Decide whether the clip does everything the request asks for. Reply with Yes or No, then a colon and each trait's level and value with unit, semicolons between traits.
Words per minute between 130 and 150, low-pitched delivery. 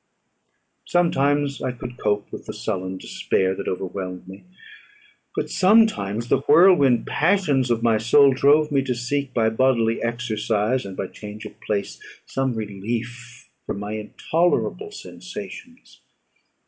Yes: slow, 135 wpm; low, 120 Hz